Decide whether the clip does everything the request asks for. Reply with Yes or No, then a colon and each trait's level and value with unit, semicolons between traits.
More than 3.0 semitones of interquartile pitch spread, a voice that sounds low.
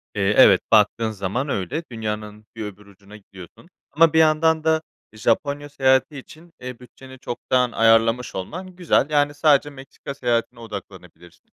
Yes: wide, 5.5 semitones; low, 125 Hz